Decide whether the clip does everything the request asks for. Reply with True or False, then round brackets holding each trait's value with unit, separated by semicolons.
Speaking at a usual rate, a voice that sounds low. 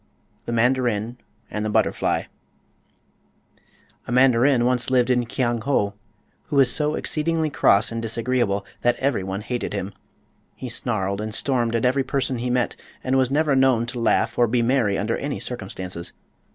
True (160 wpm; 120 Hz)